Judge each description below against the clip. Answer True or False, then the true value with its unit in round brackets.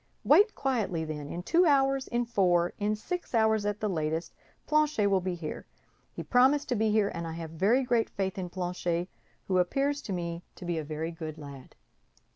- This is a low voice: False (190 Hz)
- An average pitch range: False (6.3 semitones)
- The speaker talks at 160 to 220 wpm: True (195 wpm)